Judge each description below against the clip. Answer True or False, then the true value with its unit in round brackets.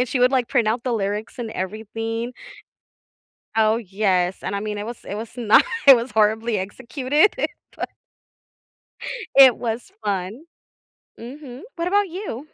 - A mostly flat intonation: False (3.3 semitones)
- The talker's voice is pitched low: False (230 Hz)